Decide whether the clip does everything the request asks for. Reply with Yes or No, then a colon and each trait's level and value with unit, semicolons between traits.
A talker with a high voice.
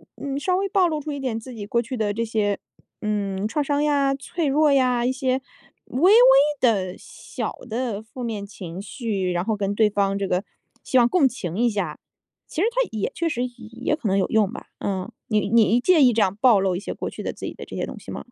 Yes: high, 235 Hz